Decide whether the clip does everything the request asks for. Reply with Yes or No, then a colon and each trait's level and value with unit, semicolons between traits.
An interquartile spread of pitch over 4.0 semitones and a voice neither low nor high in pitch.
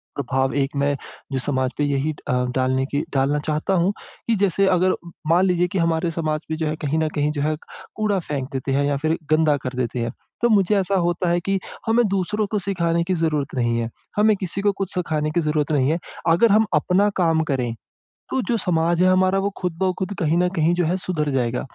Yes: average, 4.5 semitones; medium, 165 Hz